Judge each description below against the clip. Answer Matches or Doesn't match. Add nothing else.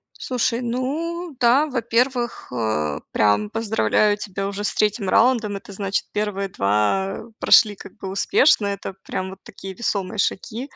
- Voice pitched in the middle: Doesn't match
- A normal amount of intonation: Matches